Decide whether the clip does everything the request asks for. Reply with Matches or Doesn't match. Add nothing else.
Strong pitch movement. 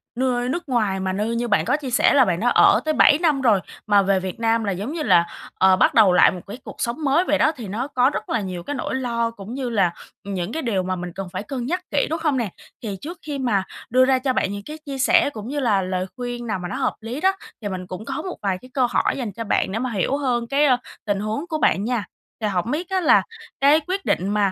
Matches